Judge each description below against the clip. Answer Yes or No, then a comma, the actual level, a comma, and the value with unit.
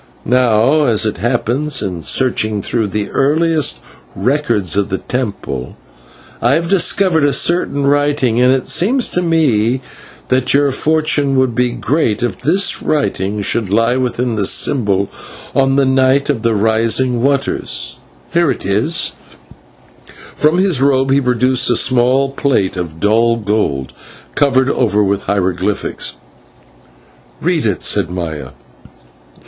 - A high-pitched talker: No, low, 125 Hz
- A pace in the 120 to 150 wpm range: Yes, average, 145 wpm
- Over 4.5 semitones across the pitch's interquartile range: Yes, average, 5.0 semitones